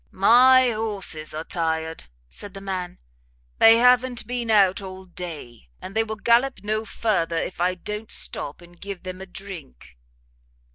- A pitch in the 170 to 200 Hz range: Yes, high, 190 Hz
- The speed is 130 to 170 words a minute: Yes, average, 155 wpm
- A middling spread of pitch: Yes, average, 4.3 semitones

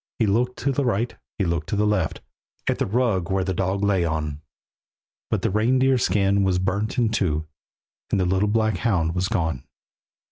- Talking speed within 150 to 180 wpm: No, average, 190 wpm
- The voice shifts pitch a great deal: No, average, 3.6 semitones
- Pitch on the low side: Yes, low, 100 Hz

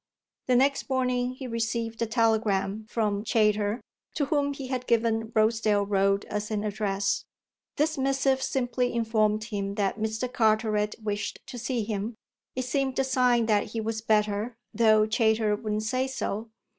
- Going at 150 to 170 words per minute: Yes, average, 155 wpm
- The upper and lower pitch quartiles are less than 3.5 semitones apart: Yes, average, 2.9 semitones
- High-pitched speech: Yes, high, 225 Hz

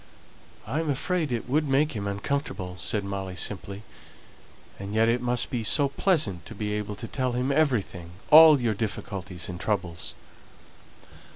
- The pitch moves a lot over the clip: Yes, wide, 5.8 semitones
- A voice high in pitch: No, low, 110 Hz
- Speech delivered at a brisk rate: No, average, 160 wpm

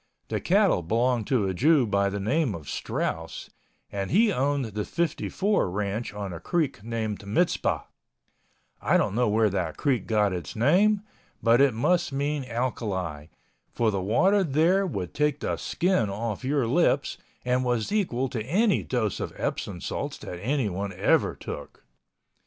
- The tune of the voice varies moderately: No, wide, 6.5 semitones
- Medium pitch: No, low, 120 Hz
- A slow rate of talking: No, average, 160 wpm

